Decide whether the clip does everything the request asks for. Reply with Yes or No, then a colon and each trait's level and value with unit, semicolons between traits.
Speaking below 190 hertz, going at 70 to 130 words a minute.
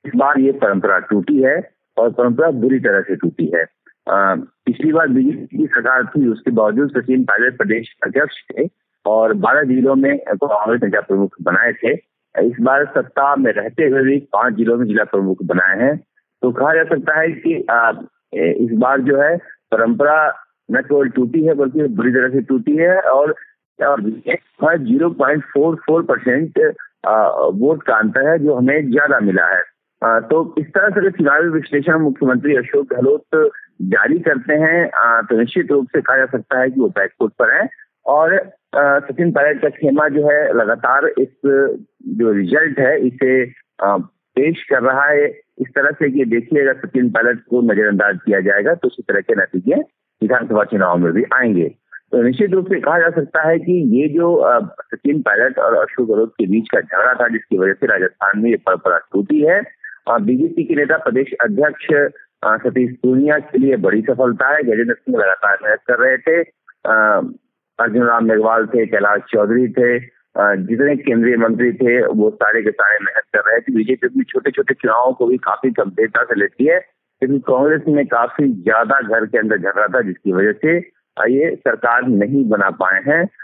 No: medium, 140 Hz; average, 185 wpm